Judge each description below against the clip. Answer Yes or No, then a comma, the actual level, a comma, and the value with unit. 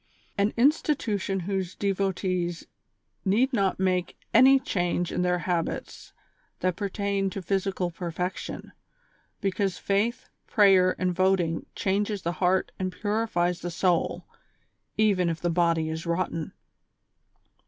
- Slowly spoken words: Yes, slow, 120 wpm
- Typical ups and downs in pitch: No, narrow, 2.3 semitones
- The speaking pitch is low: No, medium, 185 Hz